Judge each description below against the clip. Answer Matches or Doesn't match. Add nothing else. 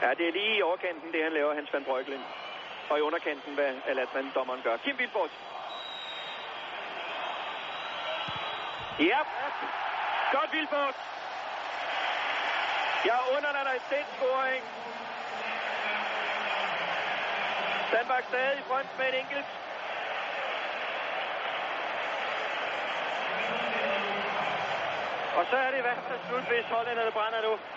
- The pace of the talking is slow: Matches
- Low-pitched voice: Doesn't match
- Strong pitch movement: Matches